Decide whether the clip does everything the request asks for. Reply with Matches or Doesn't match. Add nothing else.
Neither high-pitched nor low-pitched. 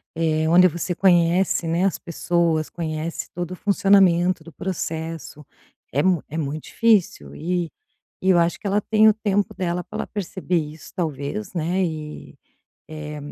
Matches